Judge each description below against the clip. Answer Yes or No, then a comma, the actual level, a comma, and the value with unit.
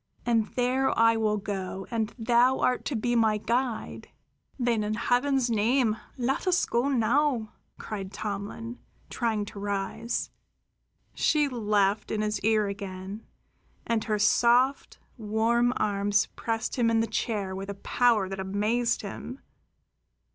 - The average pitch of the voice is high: Yes, high, 225 Hz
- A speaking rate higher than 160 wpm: No, average, 140 wpm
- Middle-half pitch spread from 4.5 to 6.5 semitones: No, average, 2.8 semitones